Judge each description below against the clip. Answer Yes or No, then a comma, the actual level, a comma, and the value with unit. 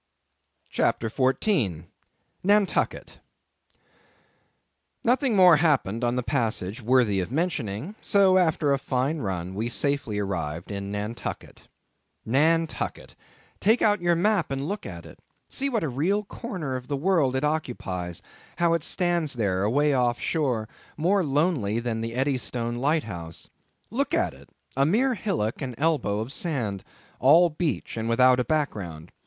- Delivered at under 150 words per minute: Yes, average, 140 wpm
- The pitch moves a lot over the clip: Yes, wide, 7.1 semitones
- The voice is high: No, low, 135 Hz